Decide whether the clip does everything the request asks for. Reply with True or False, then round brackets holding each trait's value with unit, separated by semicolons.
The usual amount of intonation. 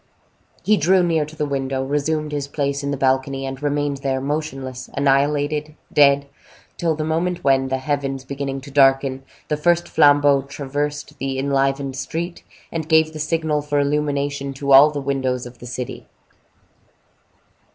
False (1.8 semitones)